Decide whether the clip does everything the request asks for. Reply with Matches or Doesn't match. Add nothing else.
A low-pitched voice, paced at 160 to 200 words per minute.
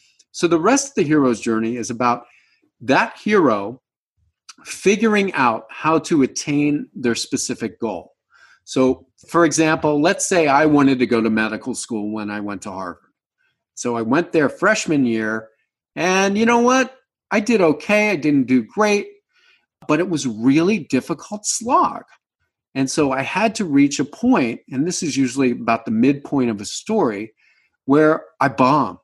Doesn't match